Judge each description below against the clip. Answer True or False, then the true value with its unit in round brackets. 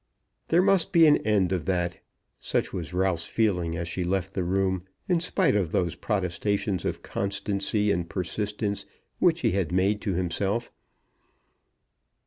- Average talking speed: True (150 wpm)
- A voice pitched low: True (95 Hz)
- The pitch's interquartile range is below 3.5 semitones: True (2.8 semitones)